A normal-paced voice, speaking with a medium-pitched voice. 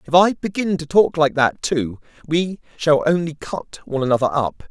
Yes: average, 190 wpm; medium, 155 Hz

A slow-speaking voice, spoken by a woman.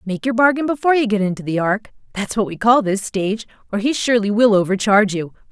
No: fast, 205 wpm; female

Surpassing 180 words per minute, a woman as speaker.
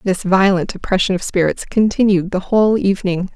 No: average, 160 wpm; female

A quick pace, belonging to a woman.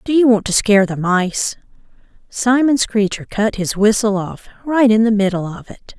No: average, 190 wpm; female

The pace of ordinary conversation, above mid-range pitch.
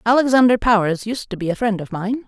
No: fast, 235 wpm; high, 215 Hz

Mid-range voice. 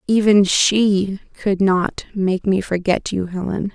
No: high, 195 Hz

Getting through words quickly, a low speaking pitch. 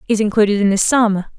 No: fast, 215 wpm; high, 210 Hz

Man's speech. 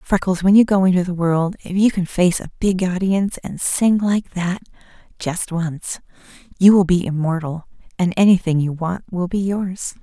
No: female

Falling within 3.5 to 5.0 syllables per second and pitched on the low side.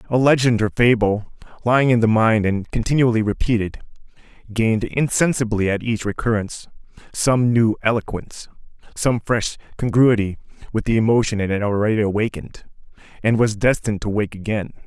No: 5.8 syllables/s; low, 110 Hz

